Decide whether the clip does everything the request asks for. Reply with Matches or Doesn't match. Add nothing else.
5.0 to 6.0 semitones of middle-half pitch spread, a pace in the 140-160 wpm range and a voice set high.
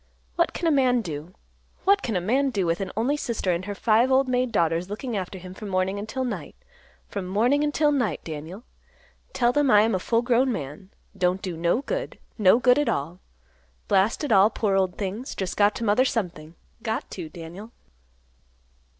Doesn't match